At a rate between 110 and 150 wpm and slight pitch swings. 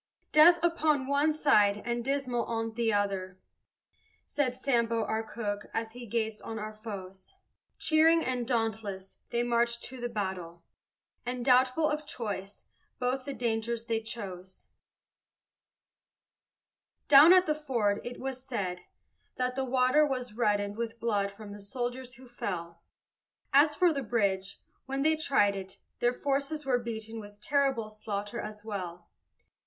No: average, 145 wpm; average, 4.3 semitones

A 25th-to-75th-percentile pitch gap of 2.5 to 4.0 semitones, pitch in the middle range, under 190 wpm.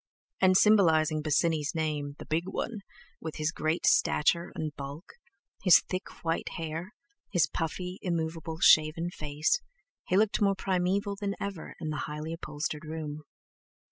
Yes: average, 3.1 semitones; medium, 165 Hz; average, 140 wpm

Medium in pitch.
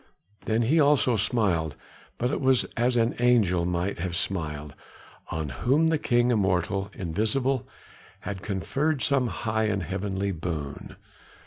No: low, 105 Hz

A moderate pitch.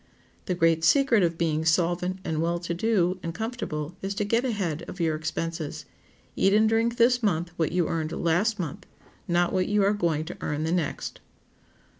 Yes: medium, 175 Hz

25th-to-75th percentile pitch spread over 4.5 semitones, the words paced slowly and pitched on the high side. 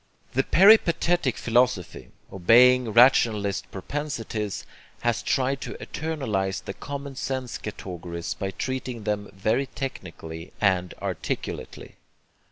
No: wide, 5.5 semitones; slow, 100 wpm; low, 115 Hz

